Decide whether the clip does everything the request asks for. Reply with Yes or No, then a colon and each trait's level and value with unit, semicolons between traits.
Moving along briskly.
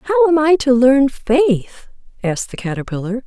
No: average, 165 wpm